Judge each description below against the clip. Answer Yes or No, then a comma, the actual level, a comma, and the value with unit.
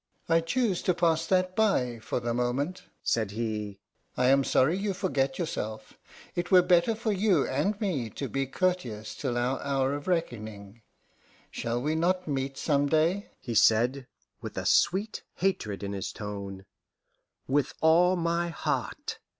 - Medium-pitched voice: Yes, medium, 145 Hz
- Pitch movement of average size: No, wide, 7.1 semitones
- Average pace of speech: Yes, average, 160 wpm